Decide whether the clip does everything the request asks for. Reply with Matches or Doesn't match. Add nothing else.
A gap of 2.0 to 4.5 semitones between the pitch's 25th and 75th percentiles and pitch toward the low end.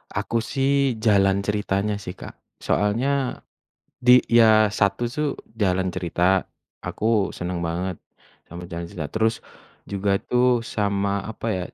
Matches